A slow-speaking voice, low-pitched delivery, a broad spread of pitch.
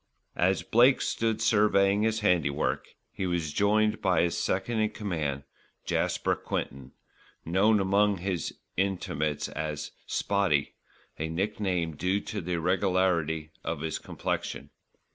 No: slow, 125 wpm; very low, 95 Hz; average, 4.3 semitones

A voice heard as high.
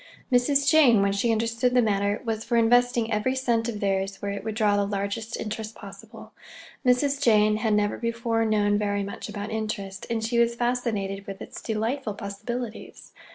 Yes: high, 220 Hz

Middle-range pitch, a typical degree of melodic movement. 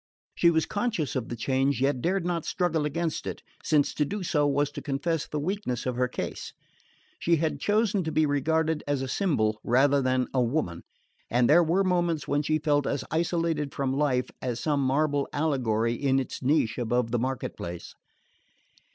Yes: medium, 145 Hz; average, 4.0 semitones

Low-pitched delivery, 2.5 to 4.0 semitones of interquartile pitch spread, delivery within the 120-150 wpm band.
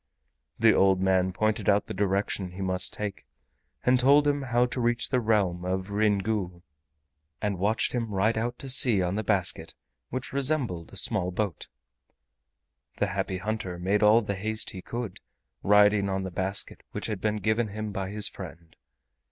No: low, 105 Hz; average, 2.8 semitones; average, 175 wpm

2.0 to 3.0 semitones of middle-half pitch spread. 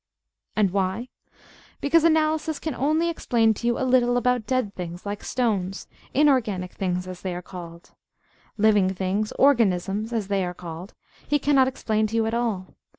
No: wide, 5.4 semitones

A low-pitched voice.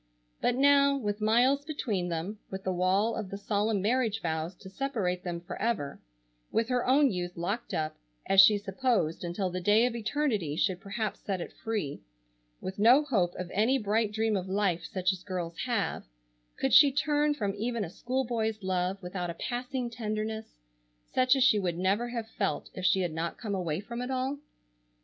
No: high, 210 Hz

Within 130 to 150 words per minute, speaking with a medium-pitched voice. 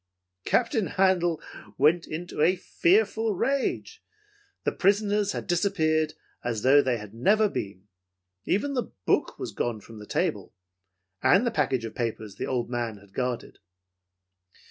Yes: average, 145 wpm; medium, 160 Hz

